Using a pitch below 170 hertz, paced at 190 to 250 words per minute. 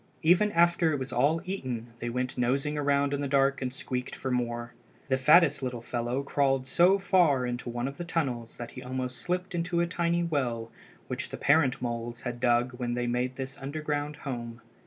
Yes: low, 135 Hz; average, 200 wpm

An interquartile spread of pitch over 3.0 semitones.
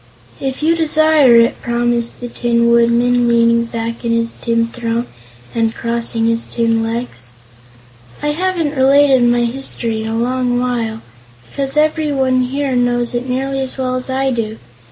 No: narrow, 2.4 semitones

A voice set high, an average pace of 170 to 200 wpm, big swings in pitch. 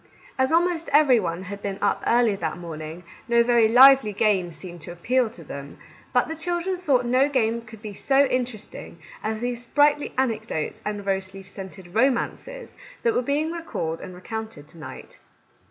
Yes: high, 225 Hz; average, 180 wpm; wide, 6.0 semitones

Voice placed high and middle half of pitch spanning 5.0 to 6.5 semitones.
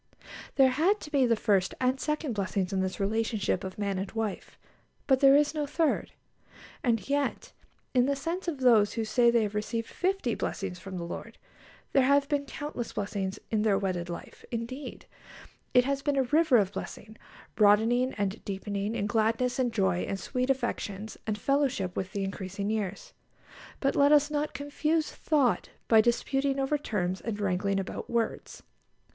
Yes: high, 230 Hz; wide, 5.5 semitones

